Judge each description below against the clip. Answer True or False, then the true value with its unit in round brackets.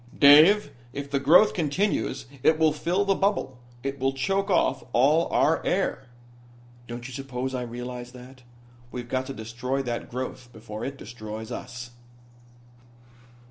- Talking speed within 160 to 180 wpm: False (145 wpm)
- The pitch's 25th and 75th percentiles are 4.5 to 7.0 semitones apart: False (3.8 semitones)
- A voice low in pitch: True (130 Hz)